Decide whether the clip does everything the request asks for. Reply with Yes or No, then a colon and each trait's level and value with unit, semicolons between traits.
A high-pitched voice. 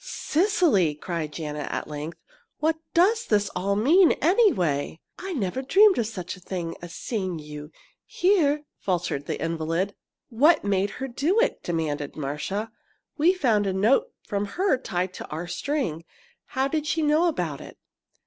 Yes: high, 205 Hz